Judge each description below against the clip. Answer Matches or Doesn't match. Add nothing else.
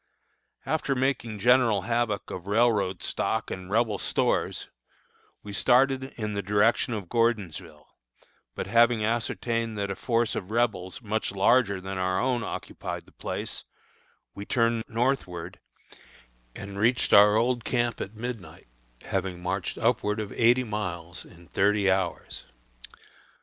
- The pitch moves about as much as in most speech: Matches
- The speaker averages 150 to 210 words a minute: Doesn't match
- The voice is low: Matches